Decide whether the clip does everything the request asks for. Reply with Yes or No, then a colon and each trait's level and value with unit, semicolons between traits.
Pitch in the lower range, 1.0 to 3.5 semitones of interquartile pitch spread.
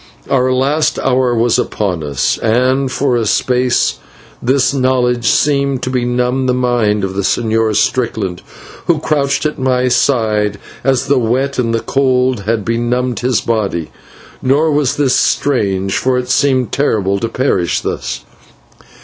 Yes: low, 125 Hz; average, 2.9 semitones